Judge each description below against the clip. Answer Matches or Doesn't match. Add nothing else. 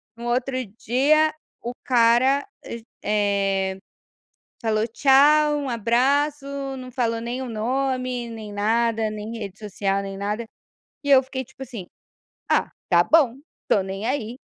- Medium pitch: Doesn't match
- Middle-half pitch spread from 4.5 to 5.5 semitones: Doesn't match